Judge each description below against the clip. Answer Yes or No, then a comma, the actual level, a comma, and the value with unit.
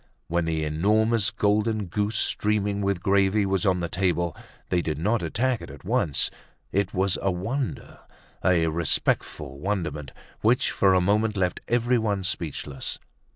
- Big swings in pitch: No, average, 3.6 semitones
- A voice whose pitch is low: Yes, very low, 95 Hz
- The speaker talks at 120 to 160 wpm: Yes, average, 150 wpm